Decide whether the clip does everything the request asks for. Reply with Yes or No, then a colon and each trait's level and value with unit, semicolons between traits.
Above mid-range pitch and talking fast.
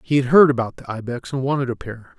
No: low, 130 Hz; fast, 275 wpm